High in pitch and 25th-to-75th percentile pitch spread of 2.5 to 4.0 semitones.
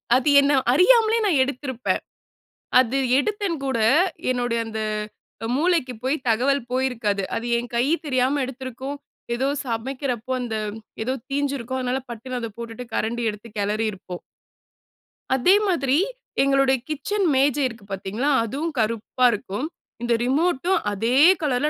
Yes: very high, 255 Hz; average, 3.3 semitones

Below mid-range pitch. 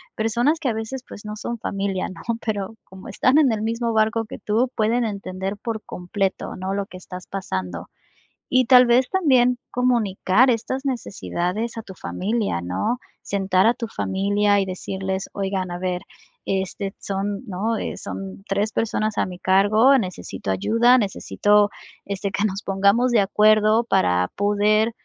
No: high, 205 Hz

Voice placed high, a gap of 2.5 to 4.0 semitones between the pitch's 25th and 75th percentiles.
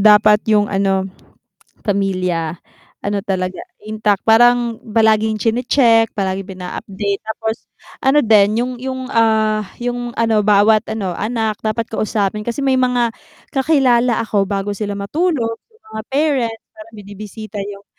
Yes: high, 220 Hz; average, 2.8 semitones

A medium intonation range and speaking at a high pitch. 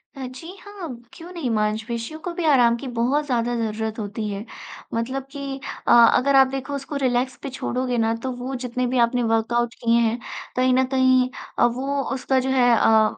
No: narrow, 2.3 semitones; very high, 250 Hz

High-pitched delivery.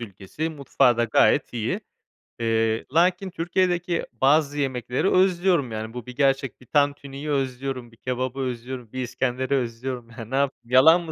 No: low, 130 Hz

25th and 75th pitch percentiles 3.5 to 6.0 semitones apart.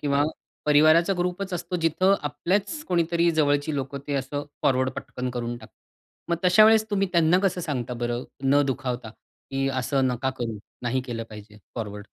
Yes: wide, 5.5 semitones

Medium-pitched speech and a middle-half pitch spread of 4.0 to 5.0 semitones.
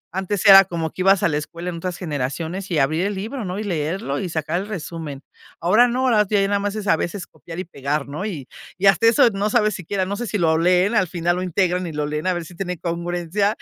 No: medium, 180 Hz; average, 3.4 semitones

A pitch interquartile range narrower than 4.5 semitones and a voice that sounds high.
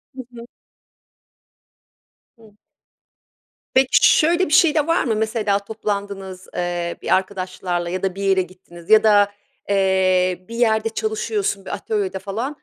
Yes: average, 3.0 semitones; high, 200 Hz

